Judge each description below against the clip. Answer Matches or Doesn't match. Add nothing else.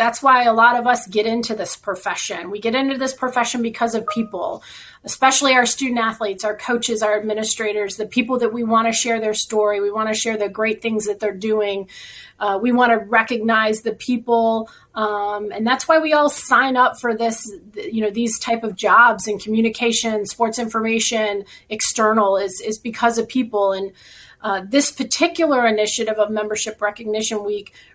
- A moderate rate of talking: Matches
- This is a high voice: Matches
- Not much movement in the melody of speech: Matches